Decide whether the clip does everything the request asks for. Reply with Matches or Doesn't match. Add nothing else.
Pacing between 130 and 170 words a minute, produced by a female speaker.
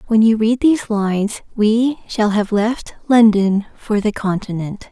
Matches